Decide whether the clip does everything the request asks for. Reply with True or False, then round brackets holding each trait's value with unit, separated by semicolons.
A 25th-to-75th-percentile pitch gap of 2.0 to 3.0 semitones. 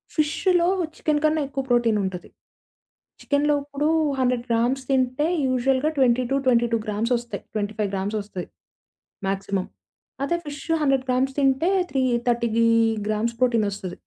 False (3.7 semitones)